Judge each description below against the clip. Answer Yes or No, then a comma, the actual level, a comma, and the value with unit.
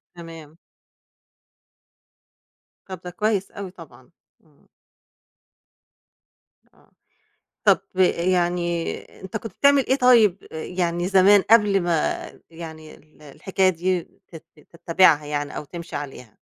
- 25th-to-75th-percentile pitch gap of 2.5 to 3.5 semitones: Yes, average, 3.1 semitones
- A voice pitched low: No, medium, 175 Hz